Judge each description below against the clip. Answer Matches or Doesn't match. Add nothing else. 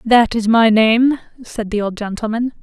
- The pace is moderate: Matches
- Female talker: Matches